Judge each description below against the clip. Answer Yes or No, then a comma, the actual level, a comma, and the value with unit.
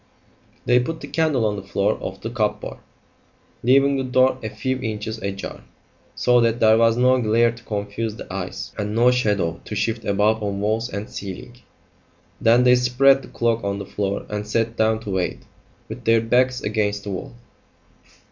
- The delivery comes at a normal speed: Yes, average, 185 wpm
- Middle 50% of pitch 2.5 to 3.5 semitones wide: Yes, average, 3.1 semitones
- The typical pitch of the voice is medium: No, low, 110 Hz